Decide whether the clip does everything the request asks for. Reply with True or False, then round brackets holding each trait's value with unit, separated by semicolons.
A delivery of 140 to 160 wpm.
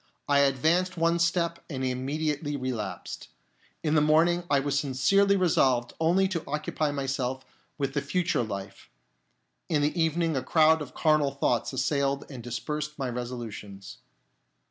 True (145 wpm)